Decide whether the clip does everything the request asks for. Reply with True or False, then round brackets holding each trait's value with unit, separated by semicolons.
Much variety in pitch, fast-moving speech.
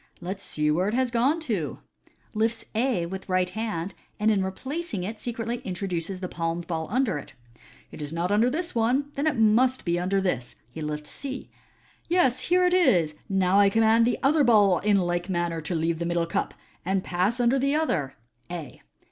True (5.8 semitones; 215 wpm)